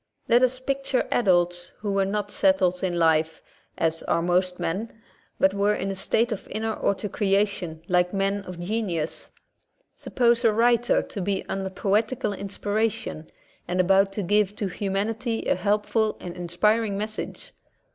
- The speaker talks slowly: No, average, 155 wpm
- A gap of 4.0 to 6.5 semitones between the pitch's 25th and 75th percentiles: No, average, 3.2 semitones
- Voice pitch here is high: Yes, high, 200 Hz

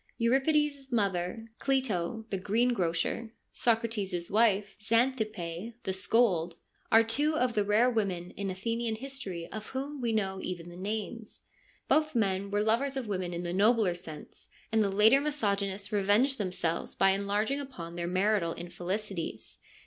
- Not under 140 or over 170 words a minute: Yes, average, 155 wpm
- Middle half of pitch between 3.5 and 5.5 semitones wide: Yes, average, 4.0 semitones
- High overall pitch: Yes, high, 210 Hz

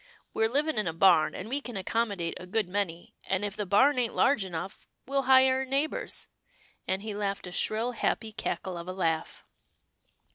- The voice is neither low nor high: No, high, 205 Hz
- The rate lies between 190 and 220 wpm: Yes, average, 195 wpm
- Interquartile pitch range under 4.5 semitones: No, average, 5.2 semitones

